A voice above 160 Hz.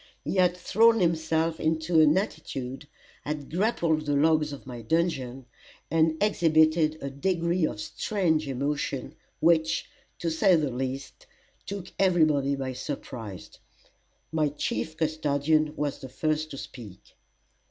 No: medium, 155 Hz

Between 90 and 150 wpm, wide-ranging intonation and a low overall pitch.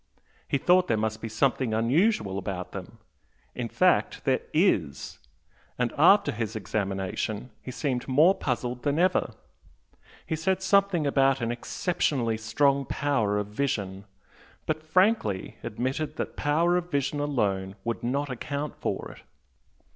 Yes: average, 140 wpm; wide, 5.9 semitones; low, 130 Hz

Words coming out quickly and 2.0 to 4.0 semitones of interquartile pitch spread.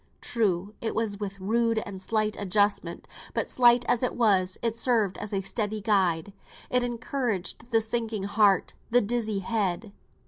No: average, 160 wpm; average, 2.9 semitones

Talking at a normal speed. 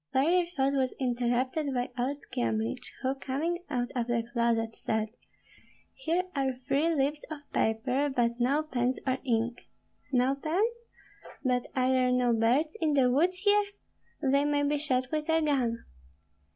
Yes: average, 155 wpm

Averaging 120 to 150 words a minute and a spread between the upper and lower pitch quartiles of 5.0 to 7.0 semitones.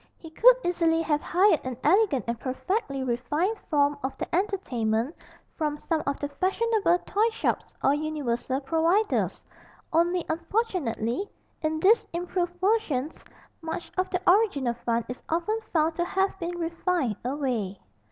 Yes: average, 140 wpm; wide, 5.4 semitones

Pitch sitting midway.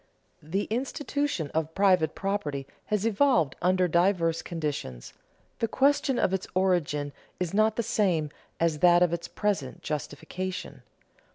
Yes: medium, 180 Hz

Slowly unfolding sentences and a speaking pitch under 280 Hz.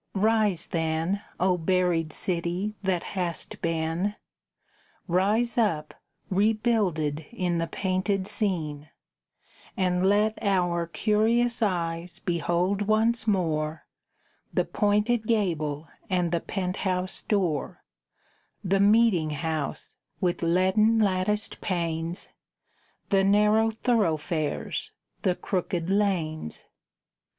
Yes: slow, 95 wpm; medium, 185 Hz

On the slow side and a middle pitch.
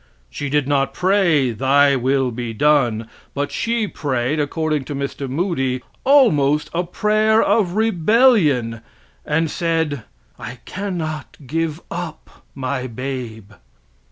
Yes: slow, 120 wpm; medium, 145 Hz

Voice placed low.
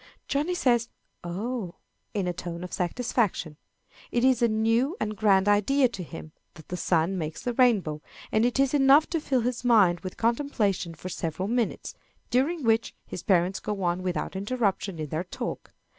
No: high, 210 Hz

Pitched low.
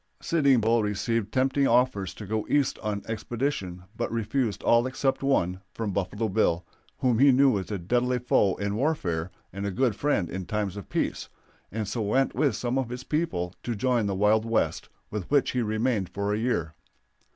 Yes: low, 110 Hz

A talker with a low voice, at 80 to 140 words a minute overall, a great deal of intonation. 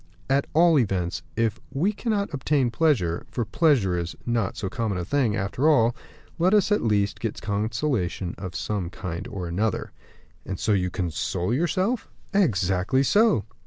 No: low, 115 Hz; average, 160 wpm; wide, 7.8 semitones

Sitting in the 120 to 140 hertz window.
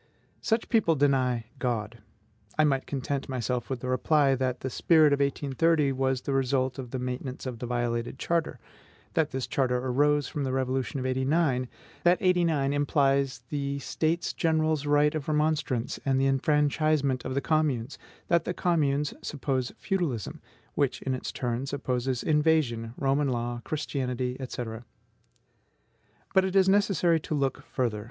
Yes: low, 135 Hz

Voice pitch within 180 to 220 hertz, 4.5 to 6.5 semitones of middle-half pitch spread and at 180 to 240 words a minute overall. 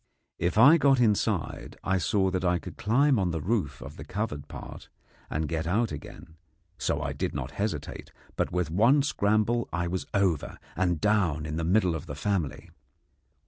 No: very low, 95 Hz; average, 5.1 semitones; average, 185 wpm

